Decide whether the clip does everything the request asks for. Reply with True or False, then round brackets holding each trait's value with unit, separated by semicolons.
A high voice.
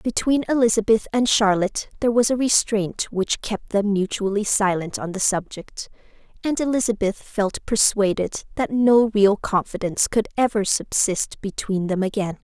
True (210 Hz)